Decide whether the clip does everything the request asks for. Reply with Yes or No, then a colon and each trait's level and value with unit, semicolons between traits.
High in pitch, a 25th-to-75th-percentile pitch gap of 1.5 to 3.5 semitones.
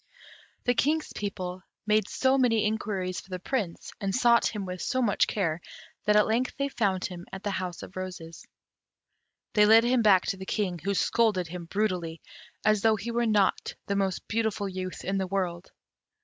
Yes: high, 200 Hz; average, 3.2 semitones